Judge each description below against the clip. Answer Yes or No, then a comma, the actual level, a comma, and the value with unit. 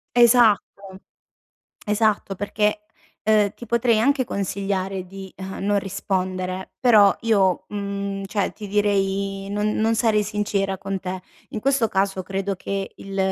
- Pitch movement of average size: No, narrow, 1.6 semitones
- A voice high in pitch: Yes, high, 200 Hz